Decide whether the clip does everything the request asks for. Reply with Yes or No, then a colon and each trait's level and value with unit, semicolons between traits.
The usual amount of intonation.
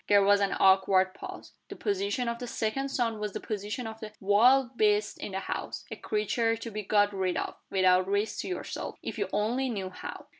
Yes: average, 3.0 semitones